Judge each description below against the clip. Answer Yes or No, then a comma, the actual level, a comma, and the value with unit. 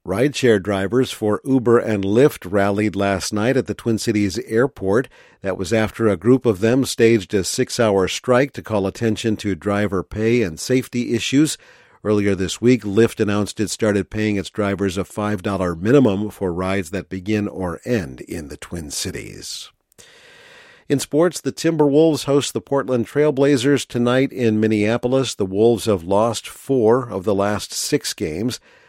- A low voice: Yes, low, 110 Hz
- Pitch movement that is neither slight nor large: Yes, average, 4.2 semitones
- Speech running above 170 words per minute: No, average, 165 wpm